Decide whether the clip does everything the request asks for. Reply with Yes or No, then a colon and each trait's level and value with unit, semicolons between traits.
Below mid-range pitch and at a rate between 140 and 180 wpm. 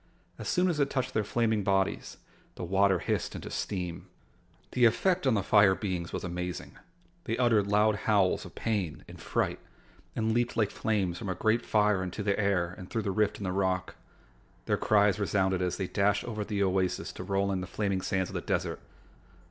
No: low, 100 Hz; average, 200 wpm